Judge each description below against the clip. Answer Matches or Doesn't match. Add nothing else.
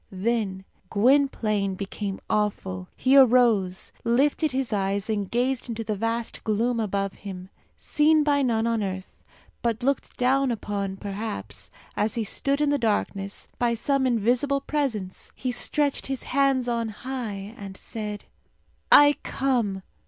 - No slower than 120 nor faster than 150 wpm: Matches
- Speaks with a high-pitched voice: Matches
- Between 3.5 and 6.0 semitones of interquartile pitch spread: Matches